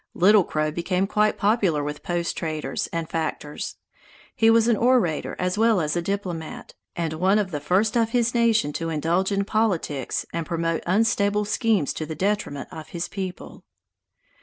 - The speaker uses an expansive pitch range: No, average, 4.7 semitones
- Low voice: No, medium, 180 Hz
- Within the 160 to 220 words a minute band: Yes, average, 170 wpm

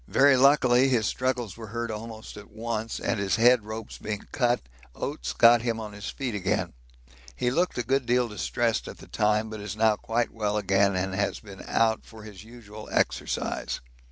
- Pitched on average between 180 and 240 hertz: No, low, 110 Hz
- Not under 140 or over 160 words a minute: No, average, 190 wpm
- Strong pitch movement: No, narrow, 2.5 semitones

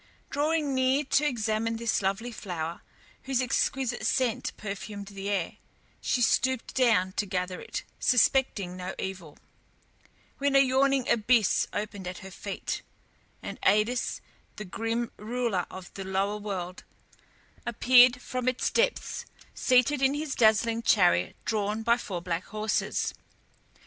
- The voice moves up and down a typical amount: Yes, average, 4.7 semitones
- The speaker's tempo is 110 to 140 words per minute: Yes, slow, 135 wpm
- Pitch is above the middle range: Yes, high, 225 Hz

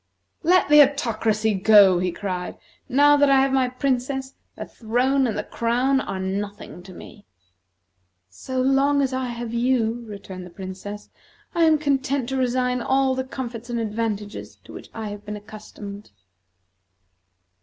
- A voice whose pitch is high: Yes, high, 240 Hz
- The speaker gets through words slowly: No, average, 155 wpm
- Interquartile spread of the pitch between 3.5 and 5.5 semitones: Yes, average, 4.4 semitones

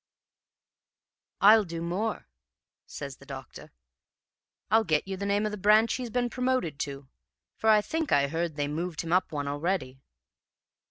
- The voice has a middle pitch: Yes, medium, 180 Hz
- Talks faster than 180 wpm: No, average, 160 wpm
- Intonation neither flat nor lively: No, wide, 6.8 semitones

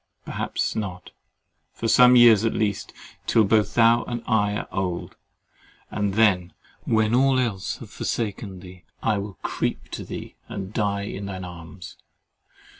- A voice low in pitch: Yes, low, 105 Hz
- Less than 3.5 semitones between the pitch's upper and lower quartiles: Yes, average, 3.1 semitones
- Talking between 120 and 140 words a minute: Yes, slow, 135 wpm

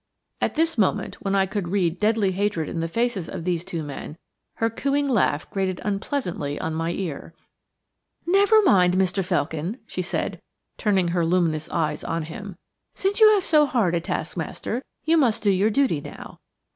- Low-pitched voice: No, high, 190 Hz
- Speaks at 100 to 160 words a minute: No, average, 175 wpm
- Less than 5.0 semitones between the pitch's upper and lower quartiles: No, average, 5.3 semitones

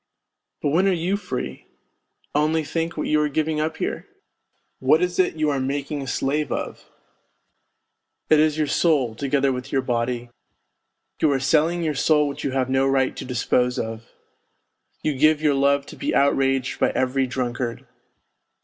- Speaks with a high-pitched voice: No, medium, 140 Hz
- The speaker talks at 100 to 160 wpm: No, average, 170 wpm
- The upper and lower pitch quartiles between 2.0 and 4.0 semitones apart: Yes, average, 2.9 semitones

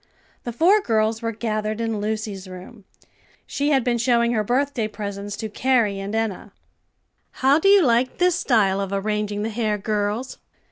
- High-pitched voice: Yes, high, 220 Hz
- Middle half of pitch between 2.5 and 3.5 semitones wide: Yes, average, 2.8 semitones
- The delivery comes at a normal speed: Yes, average, 170 wpm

